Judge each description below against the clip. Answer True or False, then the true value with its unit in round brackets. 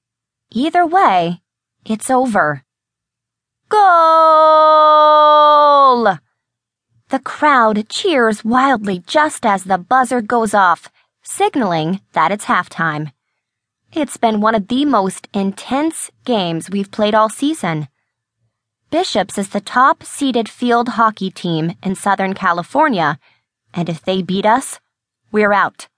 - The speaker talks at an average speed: False (115 wpm)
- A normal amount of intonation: False (8.0 semitones)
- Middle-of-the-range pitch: False (210 Hz)